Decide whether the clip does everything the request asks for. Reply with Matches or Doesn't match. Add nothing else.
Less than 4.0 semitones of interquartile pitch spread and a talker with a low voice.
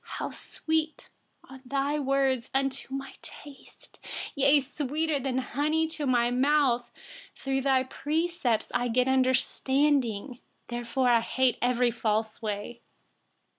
Doesn't match